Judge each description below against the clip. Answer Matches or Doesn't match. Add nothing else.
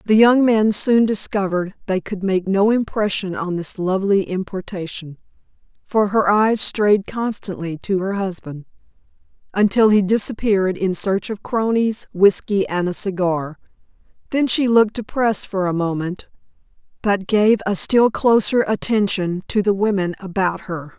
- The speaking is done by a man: Doesn't match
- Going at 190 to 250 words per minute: Doesn't match